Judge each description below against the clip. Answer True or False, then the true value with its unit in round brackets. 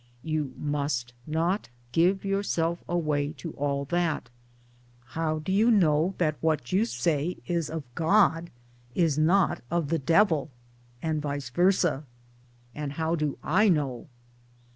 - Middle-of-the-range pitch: True (160 Hz)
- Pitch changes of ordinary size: True (3.0 semitones)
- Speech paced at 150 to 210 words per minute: False (135 wpm)